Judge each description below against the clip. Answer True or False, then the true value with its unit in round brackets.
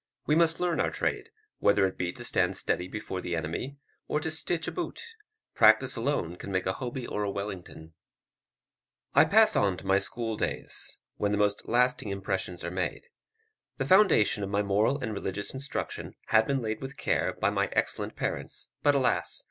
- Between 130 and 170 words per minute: False (190 wpm)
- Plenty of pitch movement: True (6.3 semitones)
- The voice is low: True (105 Hz)